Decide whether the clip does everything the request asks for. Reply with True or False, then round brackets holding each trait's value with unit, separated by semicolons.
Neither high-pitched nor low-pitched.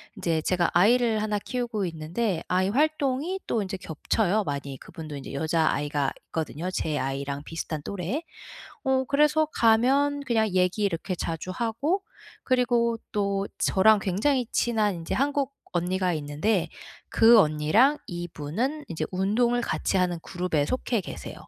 False (195 Hz)